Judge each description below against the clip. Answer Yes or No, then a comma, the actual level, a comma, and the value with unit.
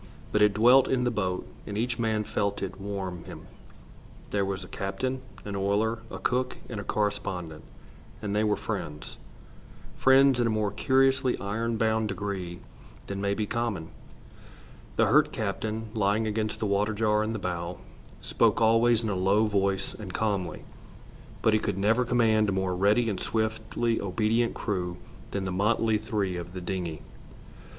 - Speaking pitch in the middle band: No, low, 105 Hz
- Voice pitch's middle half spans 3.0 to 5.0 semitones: No, narrow, 2.4 semitones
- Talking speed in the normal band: Yes, average, 170 wpm